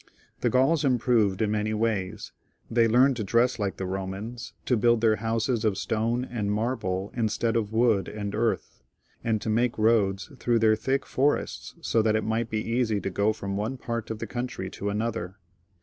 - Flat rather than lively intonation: Yes, narrow, 2.3 semitones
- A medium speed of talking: Yes, average, 190 wpm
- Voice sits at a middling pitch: No, low, 110 Hz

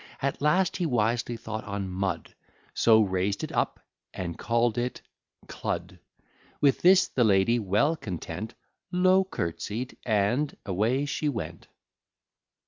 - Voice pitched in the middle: No, low, 115 Hz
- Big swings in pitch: Yes, wide, 6.1 semitones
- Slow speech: Yes, slow, 130 wpm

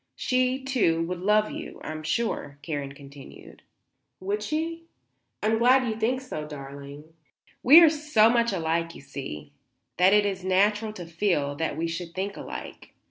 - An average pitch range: No, wide, 6.8 semitones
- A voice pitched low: No, high, 190 Hz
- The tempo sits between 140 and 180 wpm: Yes, average, 170 wpm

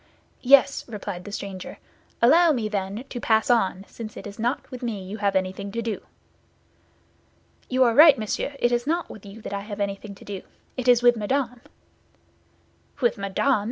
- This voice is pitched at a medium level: No, high, 220 Hz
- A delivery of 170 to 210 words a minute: Yes, average, 185 wpm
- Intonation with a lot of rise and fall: No, average, 3.6 semitones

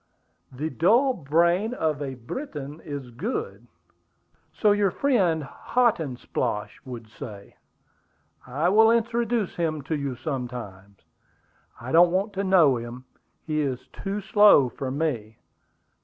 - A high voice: No, medium, 155 Hz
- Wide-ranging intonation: Yes, wide, 7.9 semitones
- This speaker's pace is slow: Yes, slow, 125 wpm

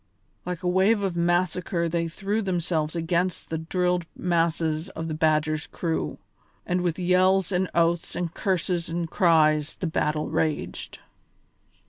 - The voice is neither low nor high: Yes, medium, 170 Hz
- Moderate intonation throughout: No, narrow, 2.1 semitones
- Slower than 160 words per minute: Yes, average, 140 wpm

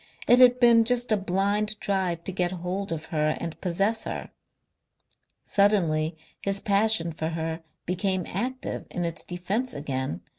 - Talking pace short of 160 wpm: Yes, average, 150 wpm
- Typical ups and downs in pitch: Yes, average, 4.2 semitones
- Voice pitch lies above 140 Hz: Yes, high, 190 Hz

